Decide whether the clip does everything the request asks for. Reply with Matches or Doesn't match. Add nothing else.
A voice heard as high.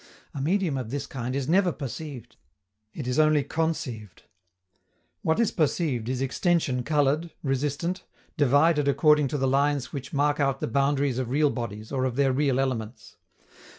Doesn't match